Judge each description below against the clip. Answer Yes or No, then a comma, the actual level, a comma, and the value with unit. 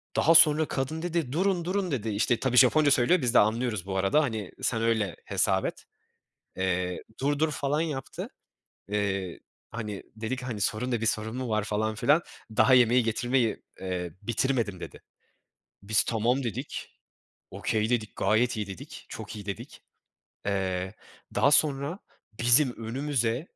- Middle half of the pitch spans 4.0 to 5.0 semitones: Yes, average, 4.6 semitones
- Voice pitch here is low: Yes, low, 120 Hz